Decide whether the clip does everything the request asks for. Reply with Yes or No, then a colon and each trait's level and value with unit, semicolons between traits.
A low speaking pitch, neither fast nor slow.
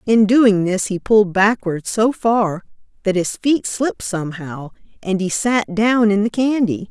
No: high, 205 Hz; average, 175 wpm